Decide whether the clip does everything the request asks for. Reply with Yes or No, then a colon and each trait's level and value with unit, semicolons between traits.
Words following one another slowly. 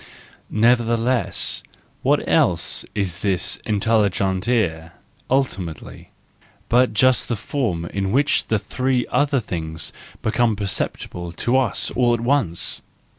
Yes: slow, 115 wpm